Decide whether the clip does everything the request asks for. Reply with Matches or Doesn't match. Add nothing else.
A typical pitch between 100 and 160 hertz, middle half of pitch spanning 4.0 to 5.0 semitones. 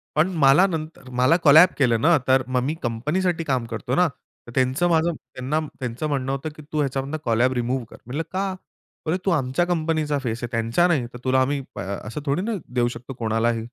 Matches